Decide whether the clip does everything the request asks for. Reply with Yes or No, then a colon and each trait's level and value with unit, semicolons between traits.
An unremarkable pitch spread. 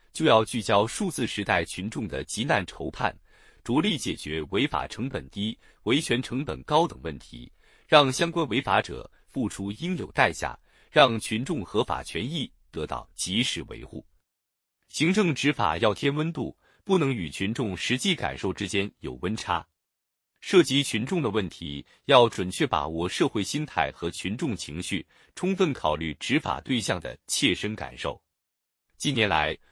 No: wide, 8.5 semitones